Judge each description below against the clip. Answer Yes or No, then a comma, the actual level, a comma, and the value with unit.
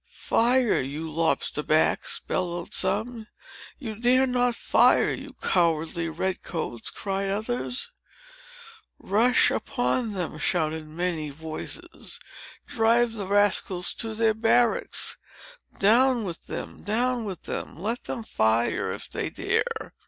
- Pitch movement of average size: No, wide, 6.2 semitones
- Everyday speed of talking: No, slow, 120 wpm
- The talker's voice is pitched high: Yes, high, 205 Hz